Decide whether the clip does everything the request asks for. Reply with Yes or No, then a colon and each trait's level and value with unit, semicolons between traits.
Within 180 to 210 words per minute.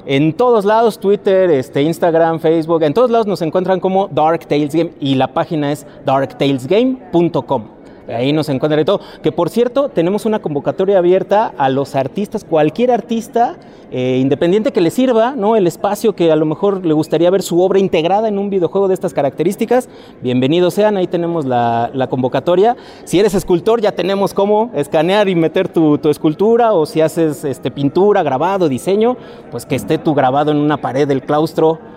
Yes: average, 185 wpm